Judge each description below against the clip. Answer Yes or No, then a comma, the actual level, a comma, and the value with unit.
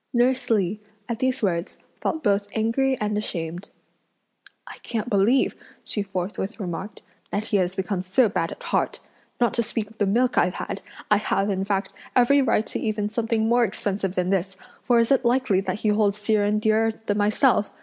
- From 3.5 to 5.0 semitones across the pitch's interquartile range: No, average, 3.1 semitones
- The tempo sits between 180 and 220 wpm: Yes, average, 190 wpm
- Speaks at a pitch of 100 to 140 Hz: No, high, 210 Hz